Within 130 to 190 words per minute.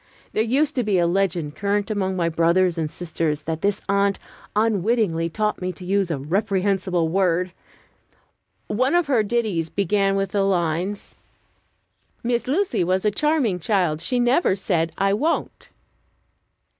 Yes: average, 150 wpm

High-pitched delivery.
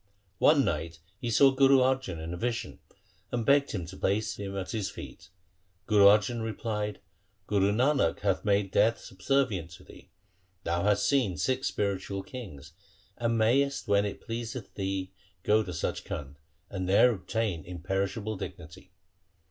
No: low, 105 Hz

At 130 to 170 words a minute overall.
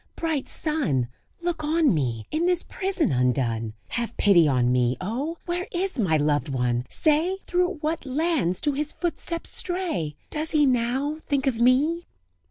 Yes: average, 165 wpm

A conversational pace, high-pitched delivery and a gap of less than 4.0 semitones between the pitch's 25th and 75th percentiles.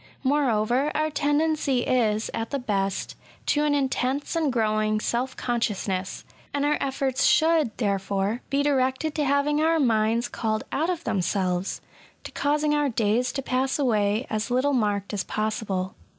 No: average, 160 wpm; very high, 250 Hz; average, 5.1 semitones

